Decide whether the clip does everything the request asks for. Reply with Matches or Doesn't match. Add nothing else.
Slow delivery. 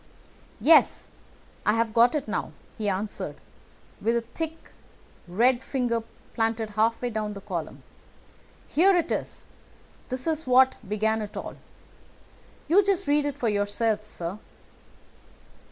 Matches